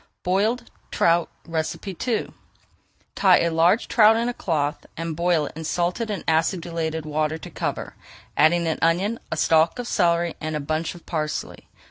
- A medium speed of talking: Yes, average, 160 wpm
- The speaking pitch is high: No, medium, 170 Hz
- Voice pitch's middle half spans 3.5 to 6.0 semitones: No, average, 2.7 semitones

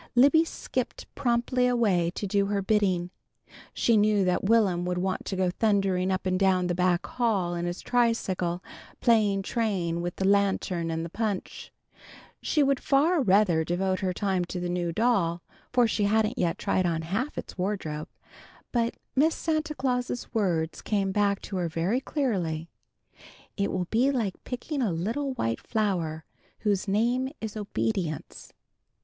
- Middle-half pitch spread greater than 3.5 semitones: Yes, average, 4.7 semitones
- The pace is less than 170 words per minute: Yes, average, 160 wpm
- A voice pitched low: No, high, 200 Hz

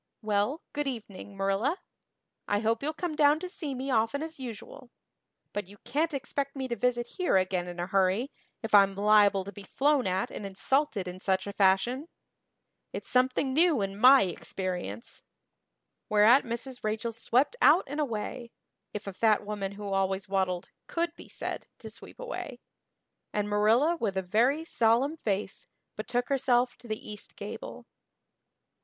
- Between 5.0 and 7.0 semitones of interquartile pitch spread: Yes, wide, 5.5 semitones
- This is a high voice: Yes, high, 225 Hz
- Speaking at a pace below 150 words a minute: No, average, 165 wpm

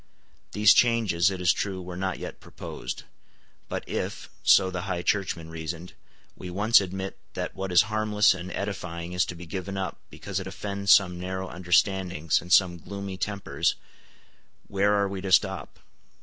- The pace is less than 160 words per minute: No, average, 165 wpm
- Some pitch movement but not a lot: No, narrow, 1.9 semitones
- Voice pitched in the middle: No, very low, 95 Hz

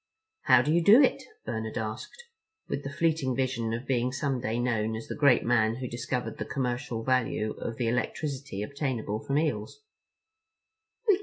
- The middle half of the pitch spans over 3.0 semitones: Yes, average, 3.7 semitones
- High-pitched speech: No, low, 125 Hz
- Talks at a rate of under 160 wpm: No, average, 165 wpm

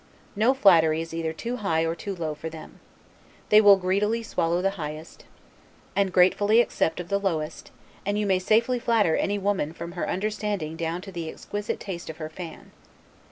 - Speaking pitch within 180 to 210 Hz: Yes, medium, 185 Hz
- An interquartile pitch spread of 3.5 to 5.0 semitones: Yes, average, 4.0 semitones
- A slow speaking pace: No, average, 185 wpm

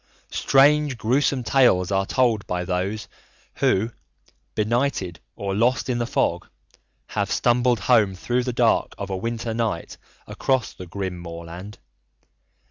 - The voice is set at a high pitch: No, low, 110 Hz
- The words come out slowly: Yes, slow, 130 wpm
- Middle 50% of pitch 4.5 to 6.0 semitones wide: Yes, average, 4.8 semitones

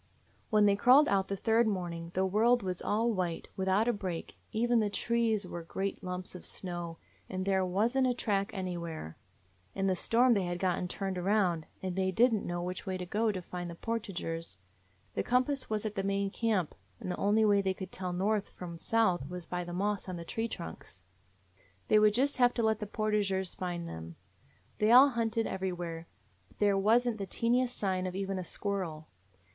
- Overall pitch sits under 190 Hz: No, high, 195 Hz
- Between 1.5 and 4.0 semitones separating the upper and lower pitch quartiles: Yes, average, 3.4 semitones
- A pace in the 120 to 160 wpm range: No, fast, 205 wpm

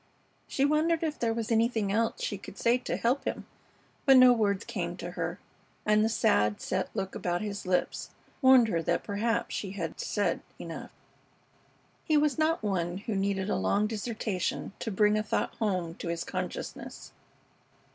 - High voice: Yes, high, 210 Hz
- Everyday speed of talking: Yes, average, 175 wpm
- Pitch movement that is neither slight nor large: Yes, average, 3.6 semitones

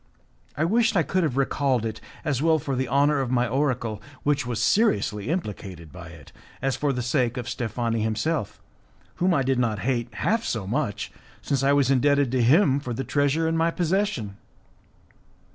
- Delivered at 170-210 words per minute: Yes, average, 185 wpm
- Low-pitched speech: Yes, low, 130 Hz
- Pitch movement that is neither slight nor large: Yes, average, 4.6 semitones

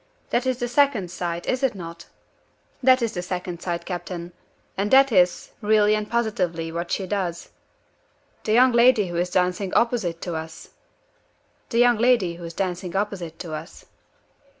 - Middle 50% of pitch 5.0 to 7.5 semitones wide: Yes, average, 5.3 semitones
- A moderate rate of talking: Yes, average, 170 wpm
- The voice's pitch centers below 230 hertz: Yes, high, 190 Hz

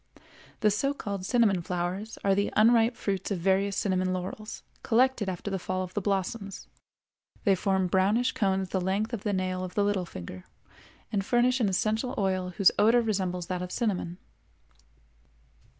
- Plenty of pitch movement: No, average, 2.7 semitones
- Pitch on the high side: Yes, high, 195 Hz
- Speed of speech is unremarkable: Yes, average, 165 wpm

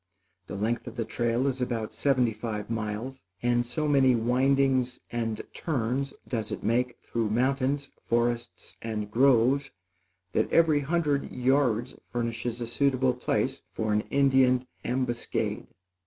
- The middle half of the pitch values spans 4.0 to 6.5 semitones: No, narrow, 2.6 semitones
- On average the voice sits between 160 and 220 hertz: No, low, 125 Hz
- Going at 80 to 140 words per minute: Yes, slow, 135 wpm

